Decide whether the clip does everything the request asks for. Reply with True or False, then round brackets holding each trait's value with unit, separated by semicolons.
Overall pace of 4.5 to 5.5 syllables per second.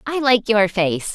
False (4.0 syllables/s)